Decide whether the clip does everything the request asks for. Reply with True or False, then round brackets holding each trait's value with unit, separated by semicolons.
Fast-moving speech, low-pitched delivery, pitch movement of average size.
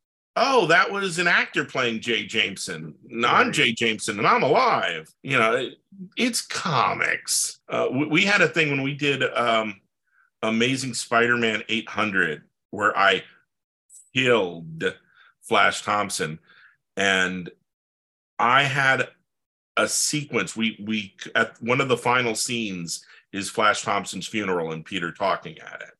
False (135 wpm; 115 Hz; 4.7 semitones)